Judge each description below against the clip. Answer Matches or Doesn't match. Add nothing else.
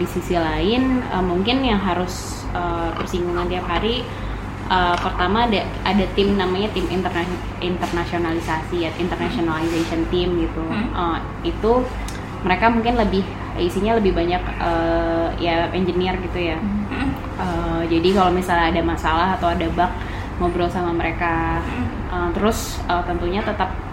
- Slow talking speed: Doesn't match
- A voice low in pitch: Doesn't match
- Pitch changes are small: Matches